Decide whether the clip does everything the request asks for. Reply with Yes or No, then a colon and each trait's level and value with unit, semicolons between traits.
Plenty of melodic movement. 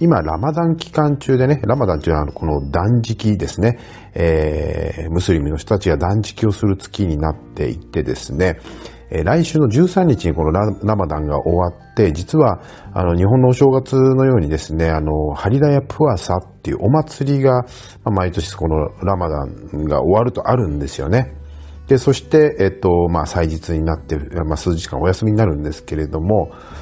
Yes: wide, 8.0 semitones